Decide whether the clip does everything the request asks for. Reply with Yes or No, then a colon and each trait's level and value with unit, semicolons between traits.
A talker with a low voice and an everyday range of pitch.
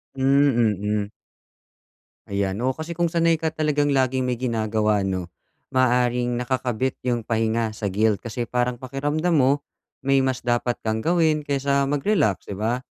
Yes: low, 125 Hz; average, 4.1 semitones